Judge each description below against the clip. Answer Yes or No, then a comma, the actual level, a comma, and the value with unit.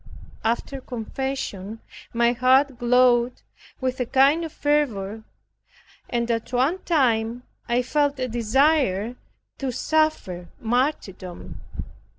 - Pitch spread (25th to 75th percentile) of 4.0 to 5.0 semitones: No, average, 3.2 semitones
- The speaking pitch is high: Yes, very high, 250 Hz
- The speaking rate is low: Yes, slow, 105 wpm